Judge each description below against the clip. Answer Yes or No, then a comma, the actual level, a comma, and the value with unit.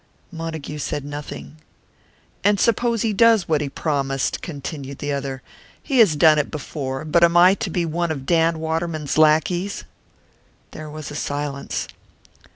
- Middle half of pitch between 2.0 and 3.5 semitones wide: Yes, average, 3.2 semitones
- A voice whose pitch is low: No, medium, 155 Hz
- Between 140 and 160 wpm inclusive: Yes, average, 155 wpm